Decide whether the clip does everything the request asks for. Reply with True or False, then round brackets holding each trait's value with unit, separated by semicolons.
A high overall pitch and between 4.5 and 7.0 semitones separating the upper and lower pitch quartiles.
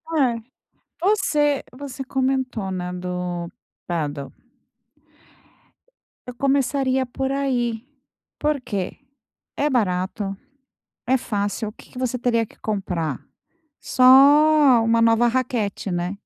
True (230 Hz; 5.6 semitones)